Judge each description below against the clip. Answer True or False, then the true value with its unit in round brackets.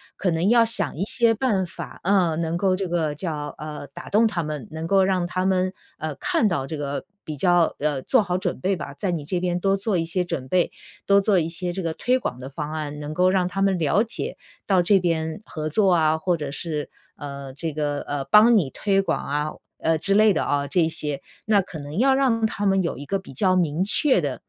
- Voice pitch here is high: False (175 Hz)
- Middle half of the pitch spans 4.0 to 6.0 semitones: True (4.3 semitones)